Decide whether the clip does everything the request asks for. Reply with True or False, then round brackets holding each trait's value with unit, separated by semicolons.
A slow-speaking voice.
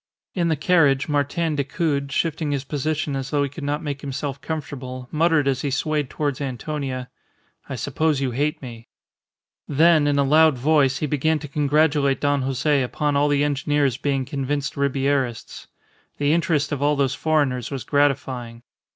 False (170 wpm)